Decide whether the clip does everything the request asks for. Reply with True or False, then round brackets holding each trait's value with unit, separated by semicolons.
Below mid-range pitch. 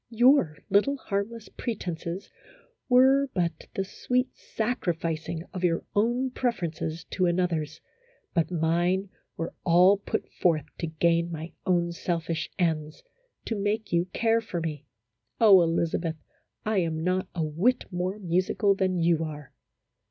False (180 Hz)